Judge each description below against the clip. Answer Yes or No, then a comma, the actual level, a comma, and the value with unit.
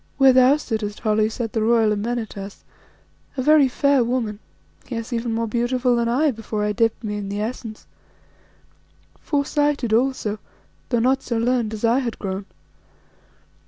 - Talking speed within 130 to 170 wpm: Yes, average, 160 wpm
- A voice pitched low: No, high, 230 Hz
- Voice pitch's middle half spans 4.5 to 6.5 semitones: No, average, 3.0 semitones